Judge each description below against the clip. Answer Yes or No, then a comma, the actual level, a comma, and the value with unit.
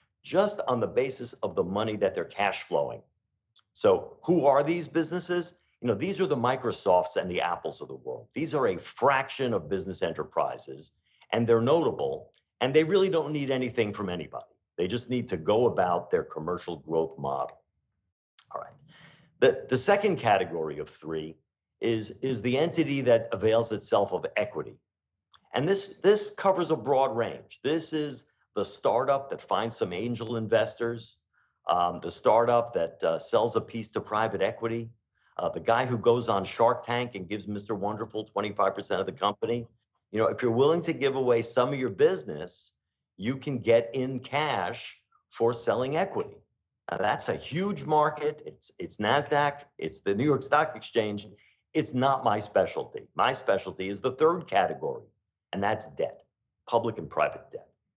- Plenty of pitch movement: Yes, wide, 6.6 semitones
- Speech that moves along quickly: No, average, 175 wpm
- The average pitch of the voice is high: No, low, 120 Hz